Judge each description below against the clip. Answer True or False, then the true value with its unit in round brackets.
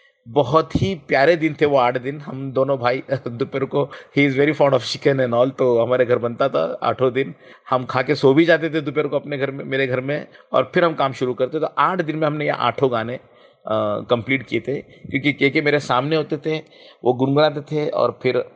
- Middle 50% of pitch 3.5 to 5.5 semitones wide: False (2.8 semitones)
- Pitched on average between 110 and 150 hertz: True (140 Hz)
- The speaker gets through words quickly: True (235 wpm)